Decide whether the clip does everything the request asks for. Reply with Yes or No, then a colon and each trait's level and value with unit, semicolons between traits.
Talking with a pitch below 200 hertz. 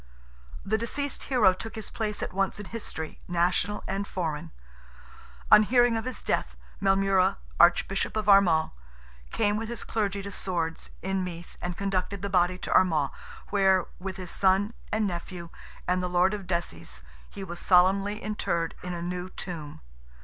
Yes: high, 190 Hz